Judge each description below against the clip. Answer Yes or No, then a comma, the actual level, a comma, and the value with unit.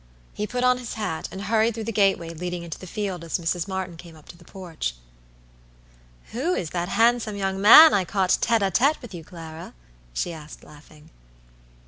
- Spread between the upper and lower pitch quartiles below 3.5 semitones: No, average, 4.6 semitones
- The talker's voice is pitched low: No, high, 190 Hz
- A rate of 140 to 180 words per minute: No, average, 195 wpm